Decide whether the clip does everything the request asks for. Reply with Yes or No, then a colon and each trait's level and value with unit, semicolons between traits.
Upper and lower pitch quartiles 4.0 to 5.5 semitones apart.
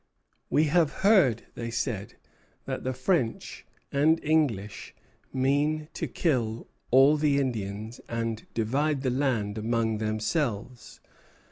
Yes: average, 4.8 semitones